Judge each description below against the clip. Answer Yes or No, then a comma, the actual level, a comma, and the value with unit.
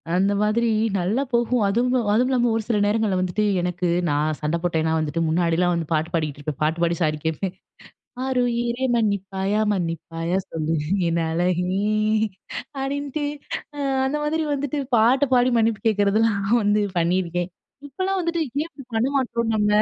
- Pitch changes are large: Yes, wide, 6.1 semitones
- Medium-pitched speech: No, high, 205 Hz